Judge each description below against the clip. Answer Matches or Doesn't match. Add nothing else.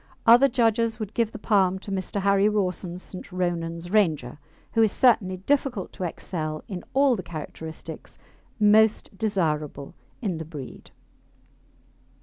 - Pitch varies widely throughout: Doesn't match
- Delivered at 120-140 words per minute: Matches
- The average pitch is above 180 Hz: Matches